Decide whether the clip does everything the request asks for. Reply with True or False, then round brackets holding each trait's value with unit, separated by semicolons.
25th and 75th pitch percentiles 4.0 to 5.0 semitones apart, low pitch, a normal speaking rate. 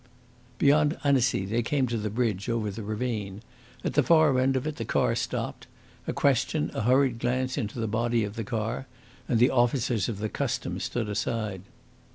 False (3.2 semitones; 115 Hz; 190 wpm)